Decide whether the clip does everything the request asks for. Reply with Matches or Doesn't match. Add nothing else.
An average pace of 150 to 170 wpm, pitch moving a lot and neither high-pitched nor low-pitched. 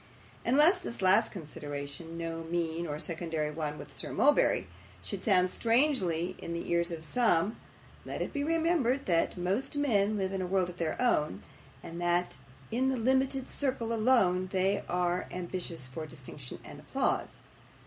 Matches